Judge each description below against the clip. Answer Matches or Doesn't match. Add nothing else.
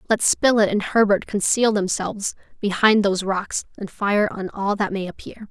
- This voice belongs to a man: Doesn't match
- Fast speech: Doesn't match